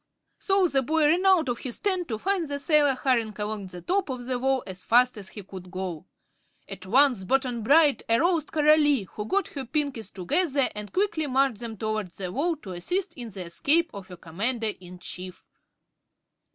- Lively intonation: Yes, wide, 7.0 semitones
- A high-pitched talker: Yes, very high, 255 Hz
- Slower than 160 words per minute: No, average, 190 wpm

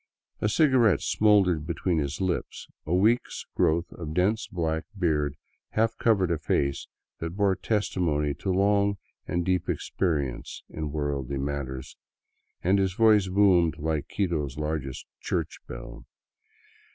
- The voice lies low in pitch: Yes, very low, 85 Hz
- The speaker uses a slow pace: Yes, slow, 130 wpm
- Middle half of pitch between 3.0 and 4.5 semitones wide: No, average, 4.9 semitones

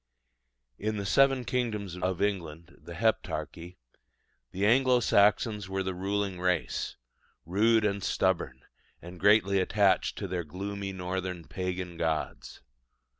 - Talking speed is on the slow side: Yes, slow, 125 wpm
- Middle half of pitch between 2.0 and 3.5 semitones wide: Yes, narrow, 2.5 semitones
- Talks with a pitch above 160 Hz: No, very low, 95 Hz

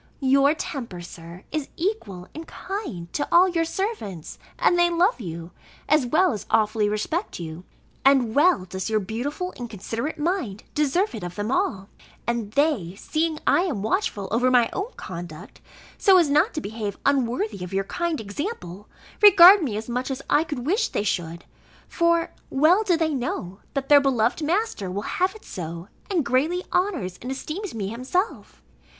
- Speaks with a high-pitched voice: Yes, very high, 265 Hz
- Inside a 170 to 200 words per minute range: Yes, average, 175 wpm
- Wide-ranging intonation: Yes, wide, 8.8 semitones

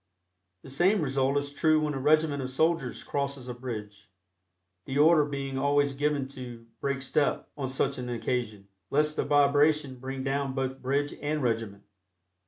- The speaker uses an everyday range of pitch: No, narrow, 2.1 semitones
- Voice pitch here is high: No, medium, 140 Hz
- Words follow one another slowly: No, average, 165 wpm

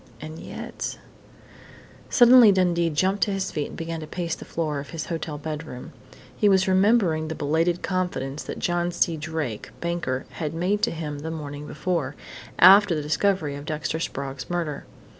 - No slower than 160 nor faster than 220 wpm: Yes, average, 170 wpm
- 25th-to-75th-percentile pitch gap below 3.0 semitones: No, average, 3.5 semitones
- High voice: No, medium, 165 Hz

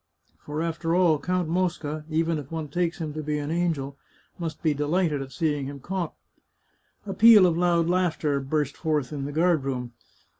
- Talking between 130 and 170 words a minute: No, average, 185 wpm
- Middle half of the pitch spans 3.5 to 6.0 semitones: No, average, 2.9 semitones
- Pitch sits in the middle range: Yes, medium, 155 Hz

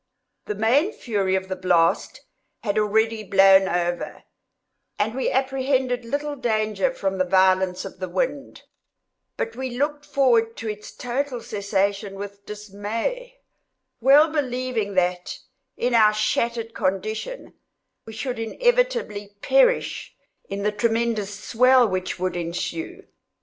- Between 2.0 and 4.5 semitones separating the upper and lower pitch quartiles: No, average, 4.9 semitones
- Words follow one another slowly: Yes, slow, 125 wpm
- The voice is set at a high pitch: Yes, high, 220 Hz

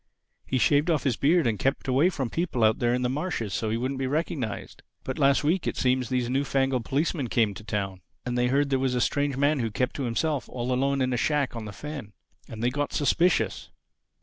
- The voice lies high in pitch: No, low, 130 Hz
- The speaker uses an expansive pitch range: No, average, 3.2 semitones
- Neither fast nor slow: No, fast, 235 wpm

